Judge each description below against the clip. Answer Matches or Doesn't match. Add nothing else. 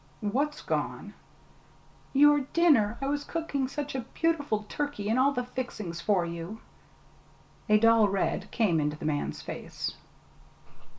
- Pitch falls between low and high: Doesn't match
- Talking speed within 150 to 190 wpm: Doesn't match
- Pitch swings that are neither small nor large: Doesn't match